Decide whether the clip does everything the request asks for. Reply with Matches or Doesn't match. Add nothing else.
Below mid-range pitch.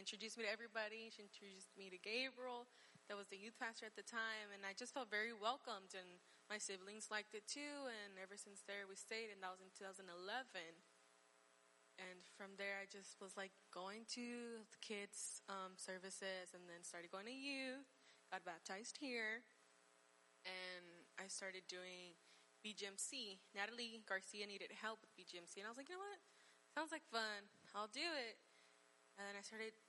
Doesn't match